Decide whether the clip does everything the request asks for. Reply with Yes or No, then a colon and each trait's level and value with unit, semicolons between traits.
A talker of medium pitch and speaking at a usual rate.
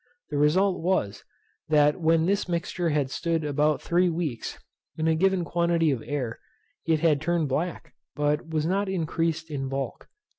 Yes: medium, 160 Hz; average, 160 wpm